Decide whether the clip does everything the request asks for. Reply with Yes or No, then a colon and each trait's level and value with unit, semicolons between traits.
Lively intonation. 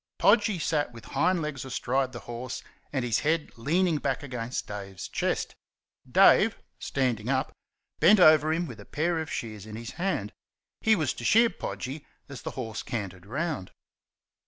Yes: wide, 5.8 semitones